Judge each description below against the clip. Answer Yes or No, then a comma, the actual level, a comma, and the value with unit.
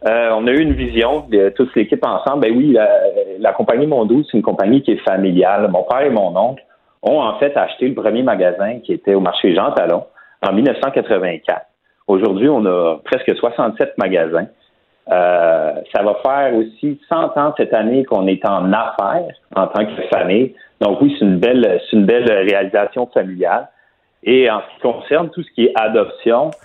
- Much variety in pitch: Yes, wide, 8.3 semitones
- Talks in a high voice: No, low, 125 Hz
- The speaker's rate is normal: Yes, average, 190 wpm